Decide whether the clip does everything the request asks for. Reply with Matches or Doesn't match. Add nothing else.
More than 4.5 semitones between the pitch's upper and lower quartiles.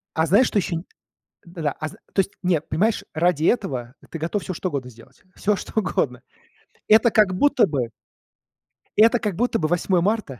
Matches